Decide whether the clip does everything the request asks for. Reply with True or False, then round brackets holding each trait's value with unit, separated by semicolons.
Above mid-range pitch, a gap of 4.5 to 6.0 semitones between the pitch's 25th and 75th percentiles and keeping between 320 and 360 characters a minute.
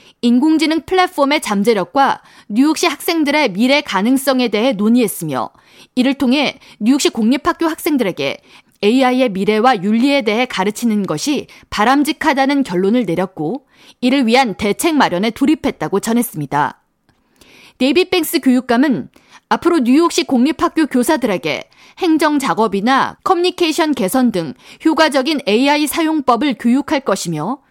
True (260 Hz; 5.4 semitones; 325 characters per minute)